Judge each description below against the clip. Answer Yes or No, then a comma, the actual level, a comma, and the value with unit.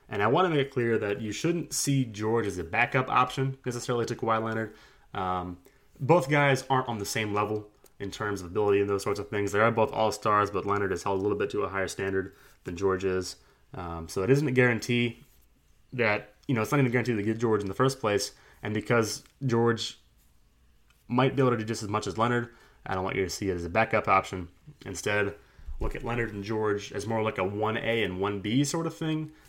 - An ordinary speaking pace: No, fast, 240 wpm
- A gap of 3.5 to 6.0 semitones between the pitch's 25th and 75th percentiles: Yes, average, 4.0 semitones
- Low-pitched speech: Yes, low, 110 Hz